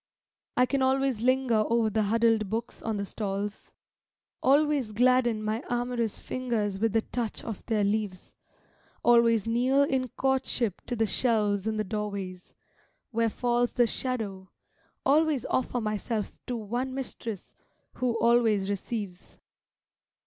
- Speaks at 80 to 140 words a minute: Yes, slow, 135 wpm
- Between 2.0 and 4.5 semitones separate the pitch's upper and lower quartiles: Yes, average, 3.0 semitones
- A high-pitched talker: Yes, high, 230 Hz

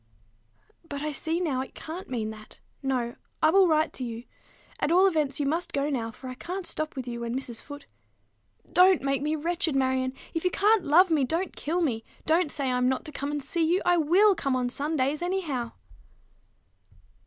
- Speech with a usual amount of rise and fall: Yes, average, 4.6 semitones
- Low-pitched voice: No, very high, 295 Hz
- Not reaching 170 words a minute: No, average, 200 wpm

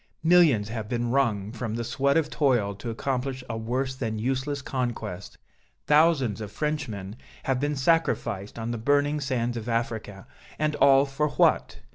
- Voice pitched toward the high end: No, low, 125 Hz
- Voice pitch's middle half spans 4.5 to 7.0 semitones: No, average, 3.9 semitones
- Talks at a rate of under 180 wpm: Yes, average, 160 wpm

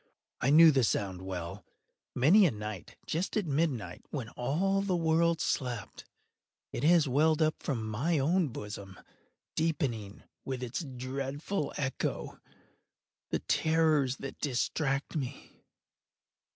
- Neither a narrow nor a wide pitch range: Yes, average, 4.9 semitones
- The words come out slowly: Yes, slow, 125 wpm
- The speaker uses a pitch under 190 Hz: Yes, medium, 140 Hz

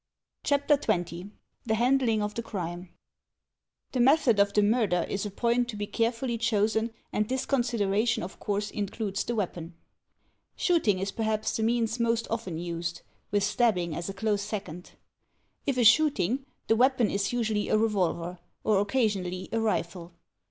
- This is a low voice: No, high, 215 Hz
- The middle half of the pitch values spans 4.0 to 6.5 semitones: No, average, 3.4 semitones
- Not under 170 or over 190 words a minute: No, average, 160 wpm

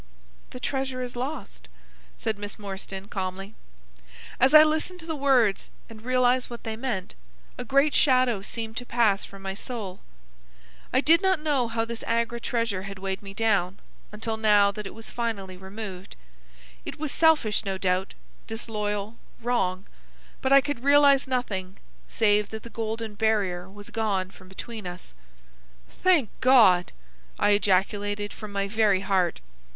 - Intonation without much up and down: No, average, 4.1 semitones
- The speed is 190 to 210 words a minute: No, average, 155 wpm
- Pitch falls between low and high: No, high, 220 Hz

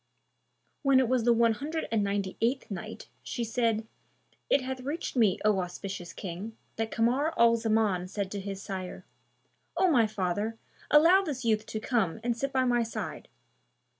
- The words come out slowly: No, average, 170 wpm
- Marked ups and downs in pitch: No, average, 4.1 semitones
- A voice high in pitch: Yes, high, 225 Hz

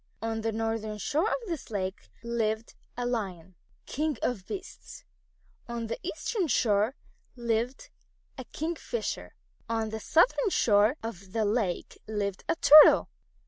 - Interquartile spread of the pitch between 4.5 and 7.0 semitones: Yes, average, 5.1 semitones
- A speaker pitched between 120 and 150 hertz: No, high, 225 Hz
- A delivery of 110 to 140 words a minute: Yes, slow, 135 wpm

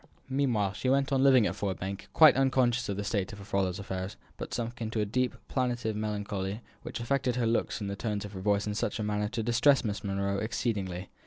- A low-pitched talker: Yes, low, 105 Hz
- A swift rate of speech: Yes, fast, 235 wpm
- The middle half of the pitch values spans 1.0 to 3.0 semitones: No, average, 3.6 semitones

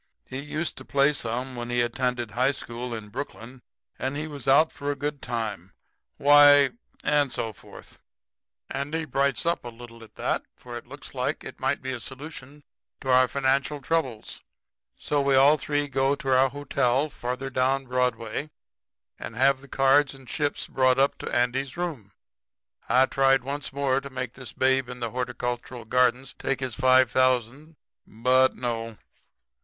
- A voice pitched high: No, low, 130 Hz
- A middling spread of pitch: No, narrow, 2.3 semitones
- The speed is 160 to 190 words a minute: Yes, average, 170 wpm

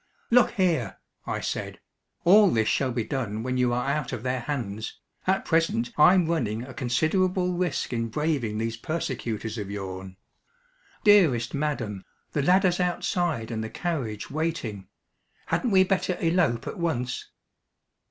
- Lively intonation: Yes, wide, 7.4 semitones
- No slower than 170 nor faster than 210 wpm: No, average, 145 wpm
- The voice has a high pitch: No, low, 135 Hz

